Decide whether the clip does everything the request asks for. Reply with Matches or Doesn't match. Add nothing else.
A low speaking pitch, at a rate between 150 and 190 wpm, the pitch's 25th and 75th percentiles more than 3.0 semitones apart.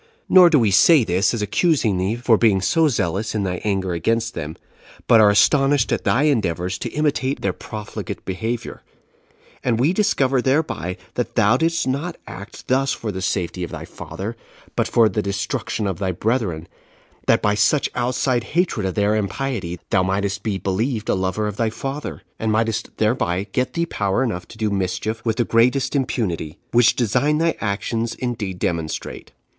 Matches